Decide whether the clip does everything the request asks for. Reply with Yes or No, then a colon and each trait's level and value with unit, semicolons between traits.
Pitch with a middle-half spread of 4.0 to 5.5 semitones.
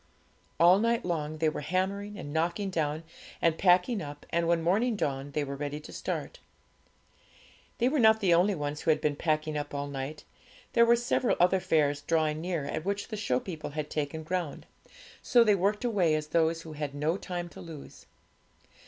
Yes: average, 4.4 semitones